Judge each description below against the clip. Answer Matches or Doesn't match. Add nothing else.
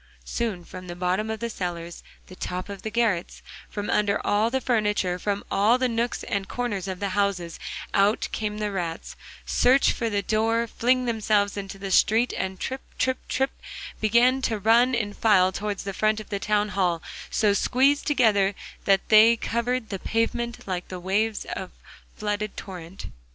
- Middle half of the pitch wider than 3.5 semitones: Doesn't match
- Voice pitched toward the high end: Matches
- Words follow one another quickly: Doesn't match